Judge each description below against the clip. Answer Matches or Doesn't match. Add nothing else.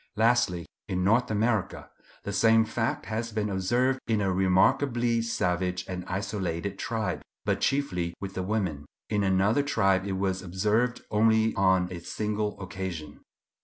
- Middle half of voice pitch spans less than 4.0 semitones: Matches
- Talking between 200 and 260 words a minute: Doesn't match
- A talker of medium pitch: Doesn't match